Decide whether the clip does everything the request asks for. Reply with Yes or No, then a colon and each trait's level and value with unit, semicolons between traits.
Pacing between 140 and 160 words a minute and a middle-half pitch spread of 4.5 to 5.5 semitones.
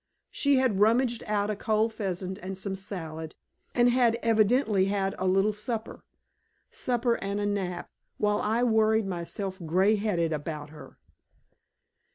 No: average, 145 wpm; average, 2.9 semitones